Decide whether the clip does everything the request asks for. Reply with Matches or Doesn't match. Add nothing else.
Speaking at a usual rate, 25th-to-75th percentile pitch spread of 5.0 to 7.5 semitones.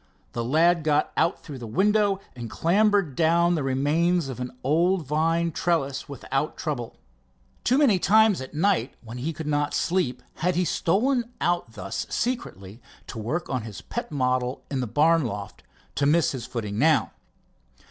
Matches